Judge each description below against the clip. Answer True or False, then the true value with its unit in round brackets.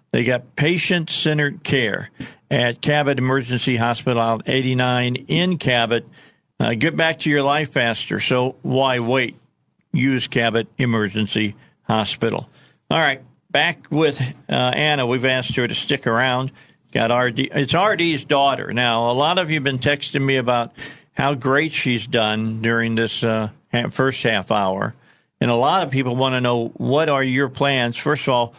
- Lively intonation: False (3.4 semitones)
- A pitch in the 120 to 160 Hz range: True (130 Hz)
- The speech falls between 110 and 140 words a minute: False (160 wpm)